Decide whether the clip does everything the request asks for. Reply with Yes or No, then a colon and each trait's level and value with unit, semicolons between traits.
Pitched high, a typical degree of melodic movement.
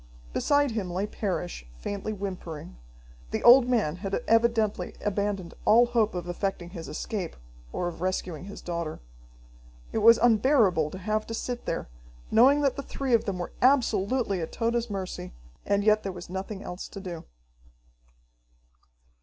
Yes: high, 200 Hz; average, 4.3 semitones